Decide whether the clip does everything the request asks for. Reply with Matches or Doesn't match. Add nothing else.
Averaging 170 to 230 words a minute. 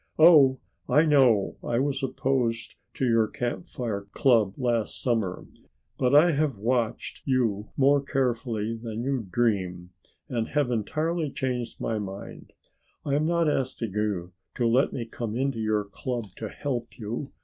Doesn't match